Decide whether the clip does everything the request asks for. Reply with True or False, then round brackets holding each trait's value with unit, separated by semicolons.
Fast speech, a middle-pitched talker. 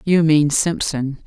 False (140 wpm; 155 Hz)